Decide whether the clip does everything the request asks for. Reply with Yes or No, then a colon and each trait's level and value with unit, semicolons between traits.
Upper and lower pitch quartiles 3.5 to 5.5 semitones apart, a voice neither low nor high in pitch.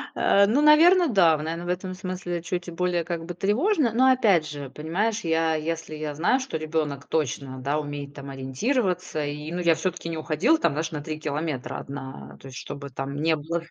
Yes: average, 4.0 semitones; medium, 165 Hz